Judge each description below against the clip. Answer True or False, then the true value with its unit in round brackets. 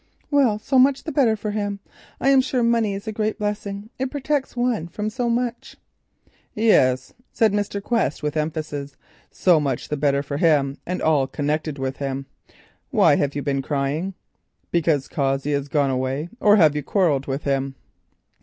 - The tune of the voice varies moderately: False (7.5 semitones)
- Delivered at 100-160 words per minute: False (175 wpm)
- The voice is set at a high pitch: False (165 Hz)